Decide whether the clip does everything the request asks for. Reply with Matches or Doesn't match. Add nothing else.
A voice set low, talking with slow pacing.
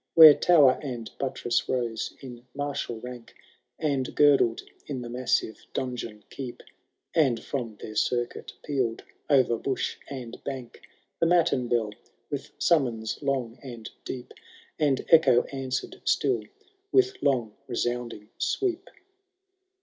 Matches